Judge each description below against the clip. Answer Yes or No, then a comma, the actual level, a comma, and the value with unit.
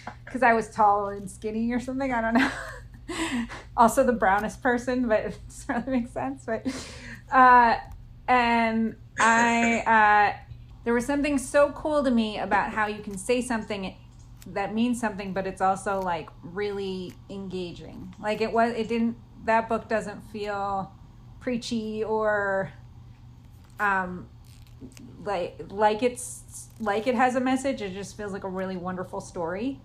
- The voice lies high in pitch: Yes, high, 215 Hz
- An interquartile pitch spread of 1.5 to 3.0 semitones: No, average, 4.0 semitones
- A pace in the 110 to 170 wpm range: Yes, average, 150 wpm